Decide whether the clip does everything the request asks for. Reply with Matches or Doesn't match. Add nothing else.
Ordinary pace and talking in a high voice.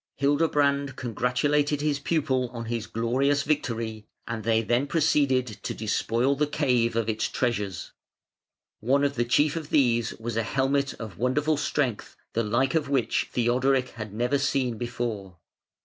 Doesn't match